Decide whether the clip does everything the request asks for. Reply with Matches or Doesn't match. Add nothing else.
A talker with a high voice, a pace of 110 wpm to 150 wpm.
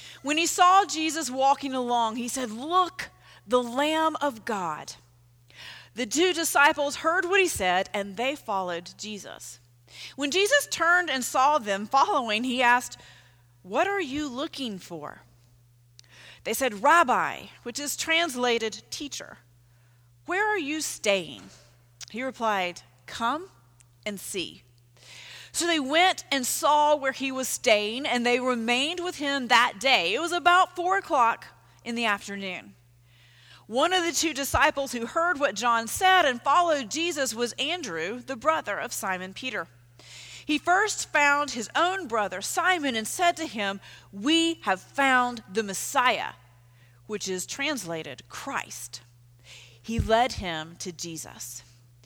Matches